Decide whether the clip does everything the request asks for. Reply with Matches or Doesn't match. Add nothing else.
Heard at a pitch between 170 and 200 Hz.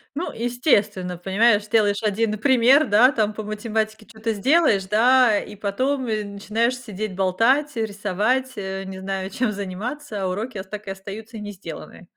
Doesn't match